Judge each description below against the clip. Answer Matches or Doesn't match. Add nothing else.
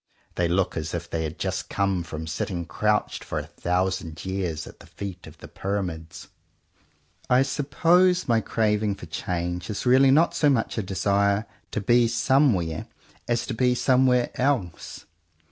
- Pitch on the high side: Doesn't match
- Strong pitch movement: Matches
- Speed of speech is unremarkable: Matches